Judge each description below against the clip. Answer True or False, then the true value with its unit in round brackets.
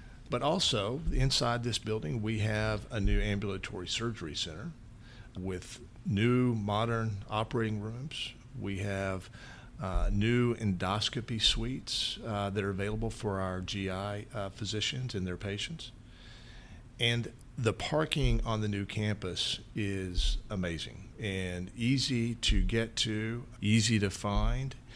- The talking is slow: True (125 wpm)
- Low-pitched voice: True (110 Hz)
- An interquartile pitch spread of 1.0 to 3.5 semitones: True (3.0 semitones)